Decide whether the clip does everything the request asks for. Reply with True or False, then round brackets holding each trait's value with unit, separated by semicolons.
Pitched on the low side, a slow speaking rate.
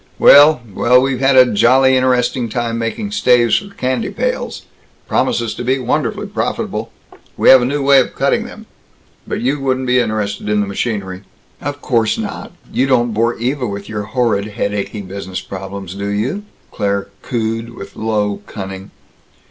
False (120 Hz; 165 wpm)